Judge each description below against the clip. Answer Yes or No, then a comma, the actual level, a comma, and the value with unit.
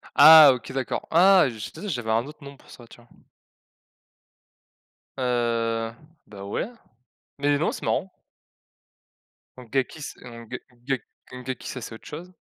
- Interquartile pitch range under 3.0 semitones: No, average, 3.7 semitones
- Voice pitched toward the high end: No, low, 125 Hz